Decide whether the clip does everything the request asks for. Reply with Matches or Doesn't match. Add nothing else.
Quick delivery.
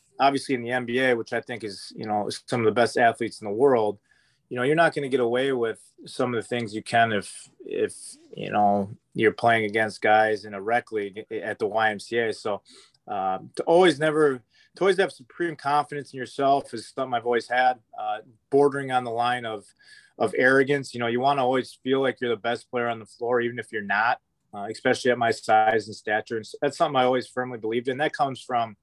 Matches